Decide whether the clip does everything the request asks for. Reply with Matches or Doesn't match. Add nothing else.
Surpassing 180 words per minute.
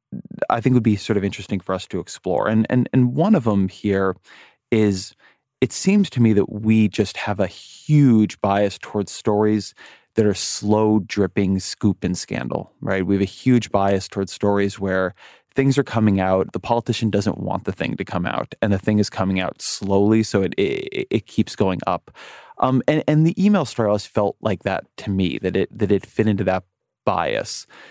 Matches